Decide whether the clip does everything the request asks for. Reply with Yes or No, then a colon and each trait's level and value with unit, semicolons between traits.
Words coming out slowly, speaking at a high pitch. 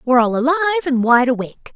No: fast, 205 wpm; very high, 270 Hz